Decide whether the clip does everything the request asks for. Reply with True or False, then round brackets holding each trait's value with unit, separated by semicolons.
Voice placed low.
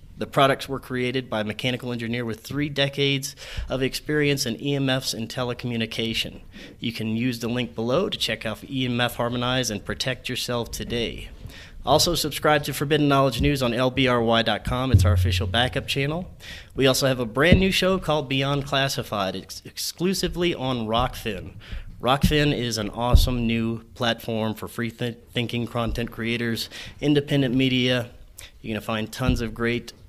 True (120 Hz)